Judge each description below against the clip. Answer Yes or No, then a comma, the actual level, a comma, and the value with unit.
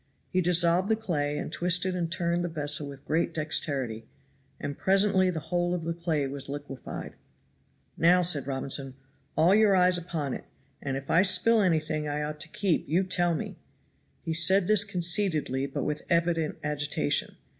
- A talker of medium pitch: Yes, medium, 165 Hz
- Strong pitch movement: No, average, 3.5 semitones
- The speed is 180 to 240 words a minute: No, average, 170 wpm